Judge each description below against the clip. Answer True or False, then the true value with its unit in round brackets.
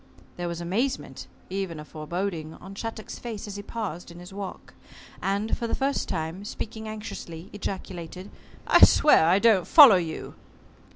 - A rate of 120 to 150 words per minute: False (160 wpm)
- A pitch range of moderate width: True (4.0 semitones)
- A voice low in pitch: False (195 Hz)